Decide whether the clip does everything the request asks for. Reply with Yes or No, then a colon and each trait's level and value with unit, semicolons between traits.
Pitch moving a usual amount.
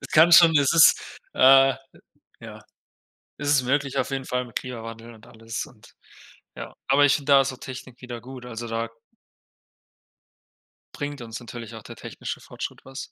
Yes: average, 3.0 semitones